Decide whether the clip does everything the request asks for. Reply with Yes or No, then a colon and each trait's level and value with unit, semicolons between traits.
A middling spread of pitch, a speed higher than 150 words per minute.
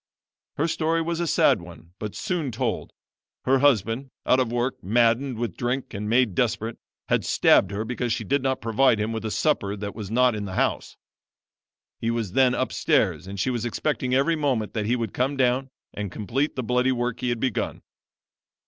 Yes: average, 3.5 semitones; average, 195 wpm